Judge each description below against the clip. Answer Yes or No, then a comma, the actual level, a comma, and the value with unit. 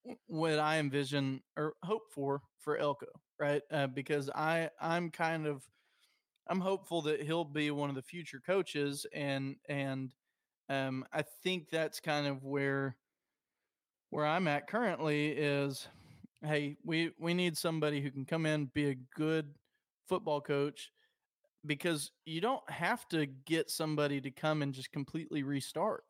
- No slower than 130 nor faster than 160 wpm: Yes, average, 150 wpm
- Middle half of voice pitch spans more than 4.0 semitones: No, average, 2.7 semitones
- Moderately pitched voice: Yes, medium, 150 Hz